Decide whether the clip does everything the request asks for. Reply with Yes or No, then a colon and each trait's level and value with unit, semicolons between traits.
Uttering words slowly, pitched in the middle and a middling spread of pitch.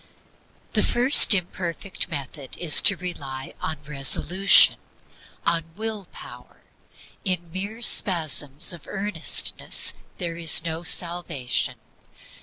Yes: slow, 105 wpm; medium, 170 Hz; average, 3.7 semitones